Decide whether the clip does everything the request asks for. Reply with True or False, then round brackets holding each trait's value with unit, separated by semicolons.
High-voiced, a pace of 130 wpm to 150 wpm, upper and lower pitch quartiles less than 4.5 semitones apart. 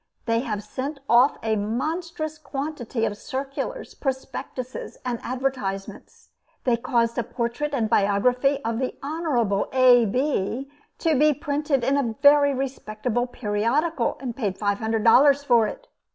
True (255 Hz; 140 wpm; 3.8 semitones)